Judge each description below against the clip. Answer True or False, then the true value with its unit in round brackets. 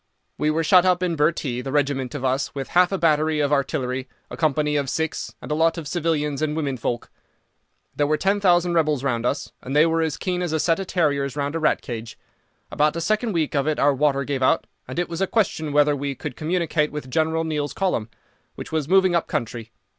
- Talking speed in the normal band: False (230 wpm)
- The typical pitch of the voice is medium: True (150 Hz)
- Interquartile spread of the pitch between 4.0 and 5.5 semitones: False (3.0 semitones)